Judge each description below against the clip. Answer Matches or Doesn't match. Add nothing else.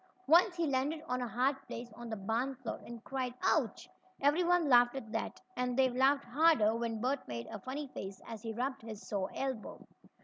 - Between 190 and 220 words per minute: Matches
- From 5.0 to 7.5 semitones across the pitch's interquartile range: Doesn't match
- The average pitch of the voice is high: Matches